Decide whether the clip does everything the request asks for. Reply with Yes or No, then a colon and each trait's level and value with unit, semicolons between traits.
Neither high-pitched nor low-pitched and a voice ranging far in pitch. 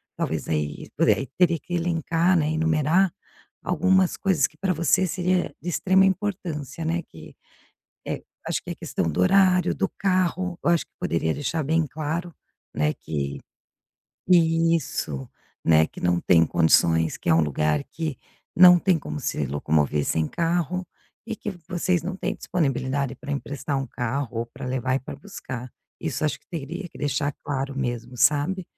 Yes: medium, 155 Hz; wide, 6.5 semitones